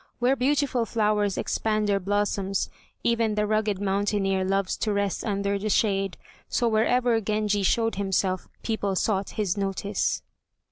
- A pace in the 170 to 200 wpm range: No, average, 140 wpm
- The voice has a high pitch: Yes, high, 205 Hz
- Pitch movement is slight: Yes, narrow, 2.0 semitones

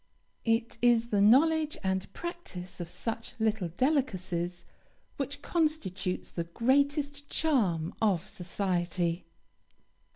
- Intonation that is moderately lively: No, wide, 7.9 semitones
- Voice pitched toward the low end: No, high, 220 Hz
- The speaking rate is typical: No, slow, 100 wpm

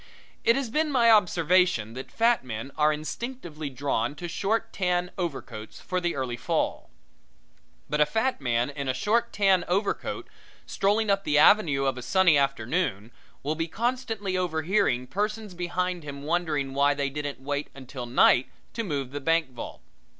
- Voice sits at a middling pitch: Yes, medium, 160 Hz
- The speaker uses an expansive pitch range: Yes, wide, 6.2 semitones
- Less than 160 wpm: No, average, 165 wpm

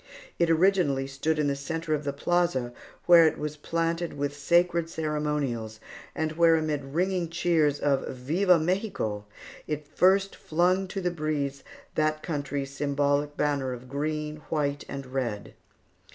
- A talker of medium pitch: Yes, medium, 150 Hz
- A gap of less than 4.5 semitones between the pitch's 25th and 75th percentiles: Yes, average, 3.1 semitones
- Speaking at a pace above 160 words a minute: No, average, 145 wpm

